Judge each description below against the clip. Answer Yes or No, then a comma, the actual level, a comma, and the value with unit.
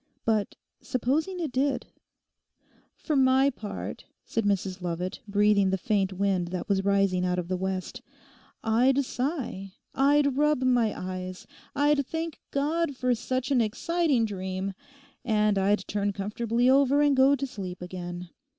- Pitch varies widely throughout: Yes, wide, 6.2 semitones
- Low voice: No, high, 220 Hz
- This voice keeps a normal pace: Yes, average, 145 wpm